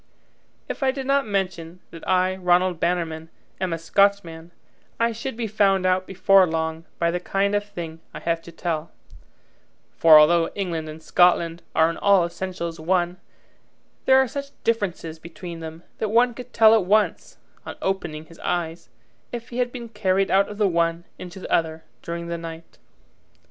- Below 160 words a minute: No, average, 175 wpm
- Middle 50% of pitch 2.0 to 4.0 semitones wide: Yes, average, 3.5 semitones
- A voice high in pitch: No, medium, 180 Hz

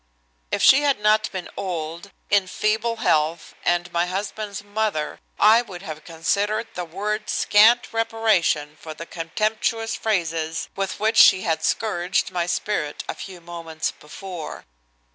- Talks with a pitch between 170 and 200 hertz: Yes, high, 190 Hz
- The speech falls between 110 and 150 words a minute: Yes, average, 145 wpm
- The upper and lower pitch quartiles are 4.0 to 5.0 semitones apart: Yes, average, 4.4 semitones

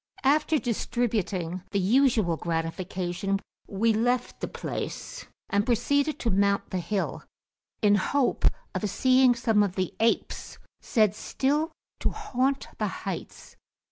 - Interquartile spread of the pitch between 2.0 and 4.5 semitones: No, average, 4.9 semitones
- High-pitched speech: Yes, high, 220 Hz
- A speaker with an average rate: No, slow, 125 wpm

